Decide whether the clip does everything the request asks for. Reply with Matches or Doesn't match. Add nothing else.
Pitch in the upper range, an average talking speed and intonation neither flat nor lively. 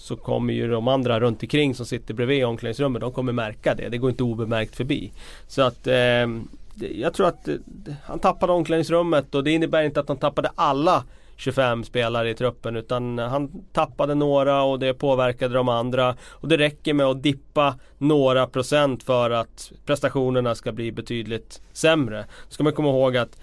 Doesn't match